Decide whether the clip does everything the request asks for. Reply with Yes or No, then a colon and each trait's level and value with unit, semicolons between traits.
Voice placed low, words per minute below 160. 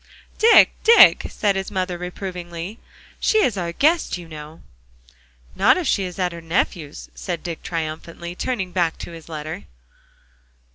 No: medium, 180 Hz; average, 150 wpm